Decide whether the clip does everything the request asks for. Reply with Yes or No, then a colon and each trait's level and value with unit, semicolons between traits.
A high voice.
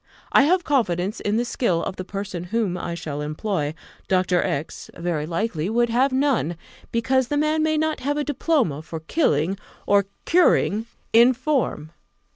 Yes: high, 215 Hz